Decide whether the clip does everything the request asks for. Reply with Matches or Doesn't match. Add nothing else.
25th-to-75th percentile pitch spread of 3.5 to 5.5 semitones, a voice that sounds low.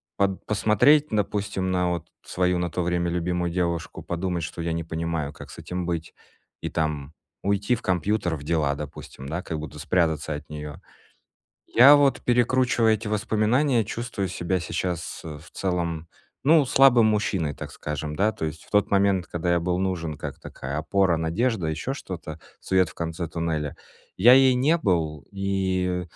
Matches